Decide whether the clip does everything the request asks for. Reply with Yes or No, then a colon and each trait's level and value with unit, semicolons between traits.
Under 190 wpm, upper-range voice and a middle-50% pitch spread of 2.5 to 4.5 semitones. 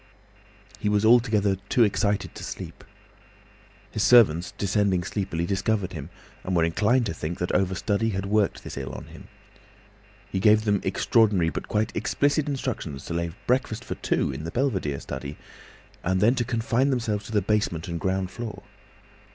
No: average, 165 wpm; low, 100 Hz; average, 3.9 semitones